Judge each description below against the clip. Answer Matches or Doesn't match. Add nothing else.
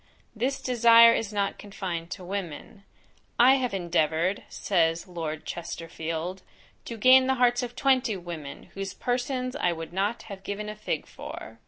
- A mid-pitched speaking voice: Doesn't match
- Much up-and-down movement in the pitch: Matches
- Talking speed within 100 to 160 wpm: Matches